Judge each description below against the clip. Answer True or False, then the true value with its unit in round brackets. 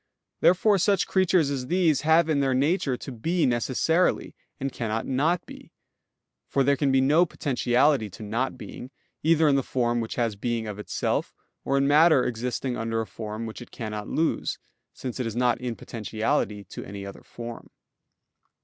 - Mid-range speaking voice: False (130 Hz)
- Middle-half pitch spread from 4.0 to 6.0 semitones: True (4.8 semitones)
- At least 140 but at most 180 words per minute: True (175 wpm)